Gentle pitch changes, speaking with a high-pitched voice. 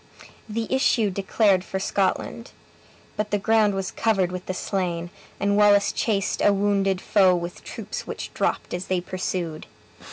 Yes: narrow, 2.1 semitones; high, 195 Hz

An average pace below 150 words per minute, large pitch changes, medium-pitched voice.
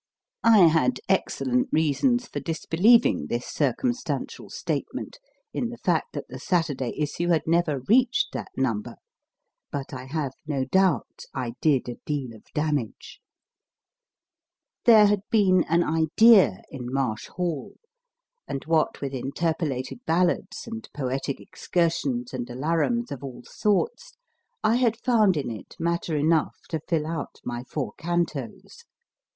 Yes: slow, 135 wpm; wide, 6.1 semitones; medium, 160 Hz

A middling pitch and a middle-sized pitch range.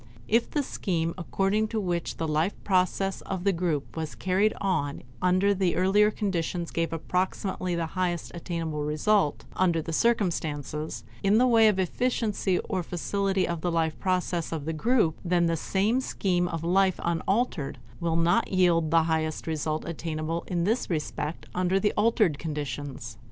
Yes: medium, 175 Hz; average, 3.2 semitones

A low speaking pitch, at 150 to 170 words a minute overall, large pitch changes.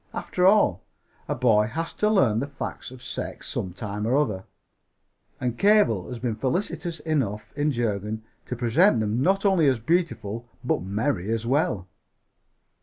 Yes: low, 120 Hz; average, 160 wpm; wide, 6.7 semitones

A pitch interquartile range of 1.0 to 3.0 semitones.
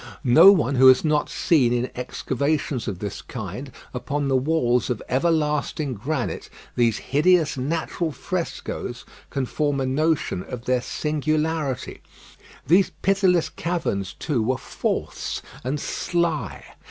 No: average, 4.0 semitones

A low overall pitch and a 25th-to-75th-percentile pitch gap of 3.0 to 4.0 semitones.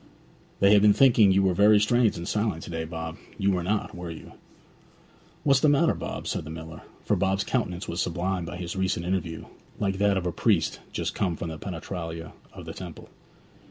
Yes: very low, 95 Hz; average, 3.4 semitones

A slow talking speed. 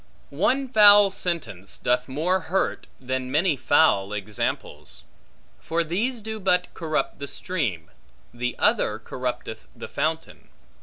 Yes: slow, 120 wpm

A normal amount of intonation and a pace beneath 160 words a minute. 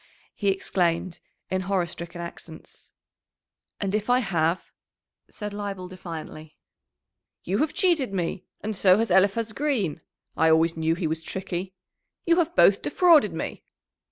Yes: average, 4.0 semitones; average, 140 wpm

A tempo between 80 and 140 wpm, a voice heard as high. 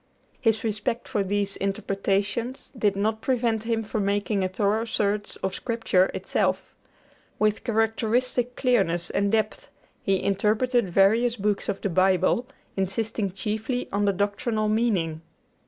Yes: slow, 135 wpm; high, 210 Hz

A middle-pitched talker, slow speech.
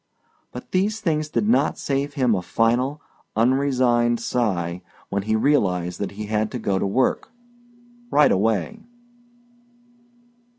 No: low, 120 Hz; slow, 130 wpm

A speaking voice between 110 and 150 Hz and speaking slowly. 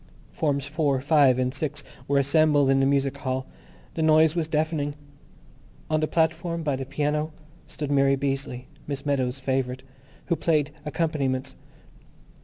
No: medium, 140 Hz; average, 145 wpm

